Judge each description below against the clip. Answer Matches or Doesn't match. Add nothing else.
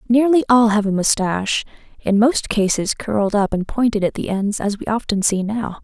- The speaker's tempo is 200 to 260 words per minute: Matches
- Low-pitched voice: Doesn't match